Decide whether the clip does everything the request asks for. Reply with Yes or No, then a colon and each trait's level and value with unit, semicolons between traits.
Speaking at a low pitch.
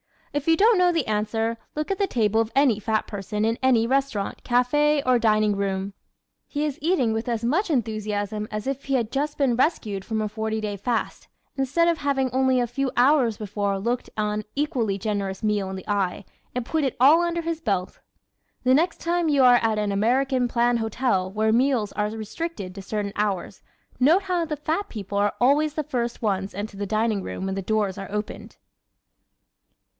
No: high, 230 Hz